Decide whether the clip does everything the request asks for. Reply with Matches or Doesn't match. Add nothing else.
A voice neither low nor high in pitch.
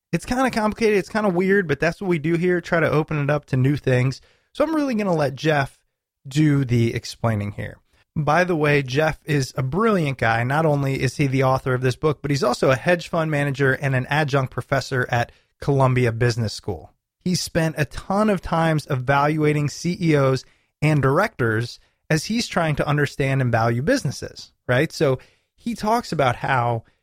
Matches